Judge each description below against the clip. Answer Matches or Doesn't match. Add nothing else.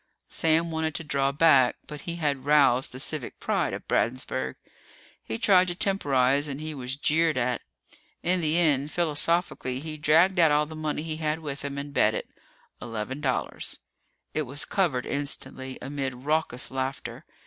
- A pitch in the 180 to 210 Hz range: Doesn't match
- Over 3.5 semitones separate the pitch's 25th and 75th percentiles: Doesn't match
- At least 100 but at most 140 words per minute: Doesn't match